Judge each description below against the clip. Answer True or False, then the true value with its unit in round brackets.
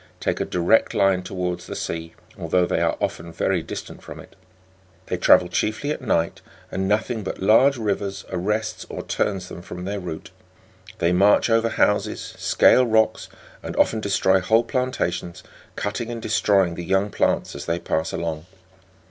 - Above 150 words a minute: True (165 wpm)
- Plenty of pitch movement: False (3.8 semitones)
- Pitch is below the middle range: True (95 Hz)